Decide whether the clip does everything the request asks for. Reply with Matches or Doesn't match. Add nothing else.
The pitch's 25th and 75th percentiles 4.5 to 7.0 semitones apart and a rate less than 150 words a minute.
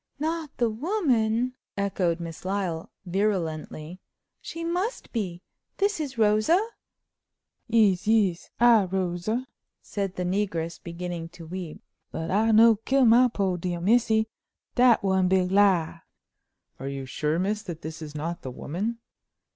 Matches